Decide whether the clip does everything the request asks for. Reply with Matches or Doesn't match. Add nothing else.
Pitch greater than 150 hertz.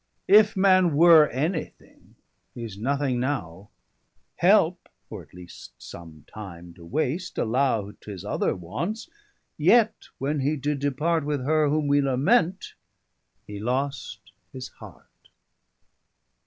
Doesn't match